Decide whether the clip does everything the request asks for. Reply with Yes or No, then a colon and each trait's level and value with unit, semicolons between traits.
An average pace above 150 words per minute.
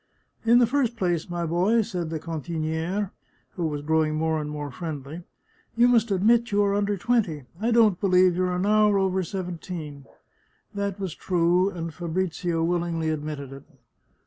Yes: average, 185 wpm